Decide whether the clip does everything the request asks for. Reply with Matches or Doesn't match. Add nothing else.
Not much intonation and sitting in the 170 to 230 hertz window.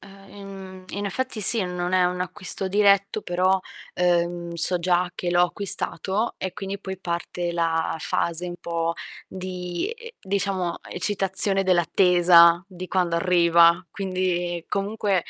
Matches